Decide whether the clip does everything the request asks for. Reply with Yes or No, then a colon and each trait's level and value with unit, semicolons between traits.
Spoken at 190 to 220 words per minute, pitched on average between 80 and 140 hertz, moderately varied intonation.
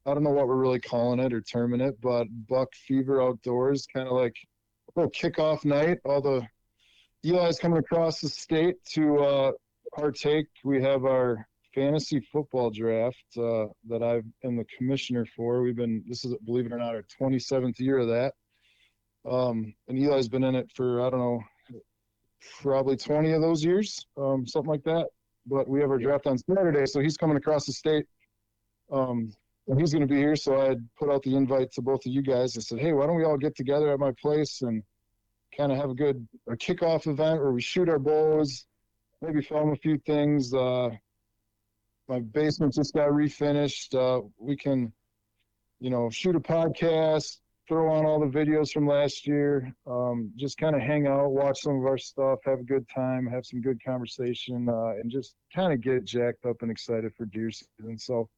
Yes: average, 200 wpm; low, 135 Hz; average, 3.7 semitones